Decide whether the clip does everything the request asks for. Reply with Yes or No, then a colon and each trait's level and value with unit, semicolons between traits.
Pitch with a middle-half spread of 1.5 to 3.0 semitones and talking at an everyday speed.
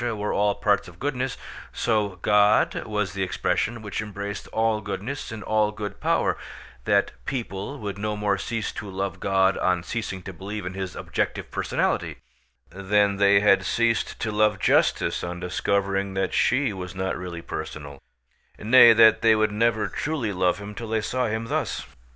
Yes: narrow, 2.4 semitones; average, 170 wpm